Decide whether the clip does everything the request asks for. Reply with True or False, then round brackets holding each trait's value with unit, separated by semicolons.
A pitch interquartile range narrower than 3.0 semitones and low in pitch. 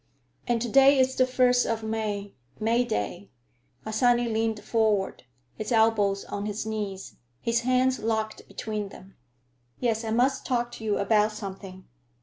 False (2.6 semitones; 220 Hz)